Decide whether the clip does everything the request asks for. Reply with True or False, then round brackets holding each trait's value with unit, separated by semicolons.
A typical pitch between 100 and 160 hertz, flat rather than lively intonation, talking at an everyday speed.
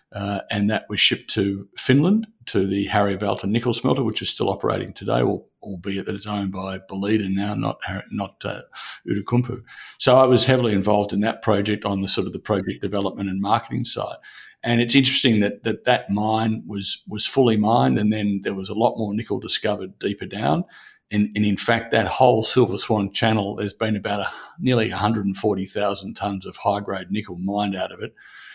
True (105 Hz; 2.1 semitones; 195 wpm)